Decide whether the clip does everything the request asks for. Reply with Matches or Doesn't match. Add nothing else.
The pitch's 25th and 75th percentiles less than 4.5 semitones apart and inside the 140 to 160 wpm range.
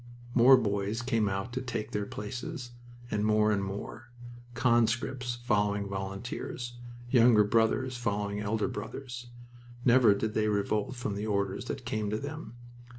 Matches